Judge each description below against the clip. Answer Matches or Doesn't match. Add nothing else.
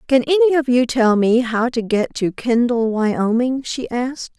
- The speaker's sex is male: Doesn't match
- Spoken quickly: Doesn't match